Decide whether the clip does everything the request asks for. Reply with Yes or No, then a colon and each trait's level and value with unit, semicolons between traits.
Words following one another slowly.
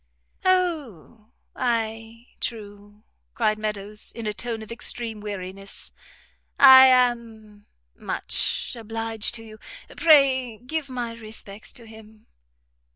Yes: slow, 105 wpm